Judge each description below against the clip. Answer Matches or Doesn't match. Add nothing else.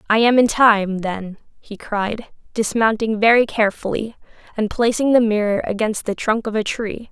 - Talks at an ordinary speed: Matches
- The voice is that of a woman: Matches